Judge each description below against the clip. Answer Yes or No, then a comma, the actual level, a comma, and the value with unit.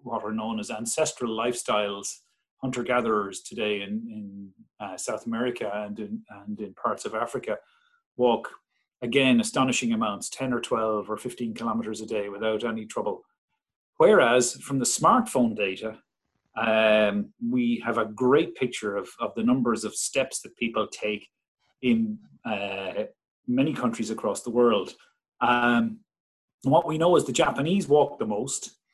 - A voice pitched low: Yes, low, 120 Hz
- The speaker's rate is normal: Yes, average, 150 wpm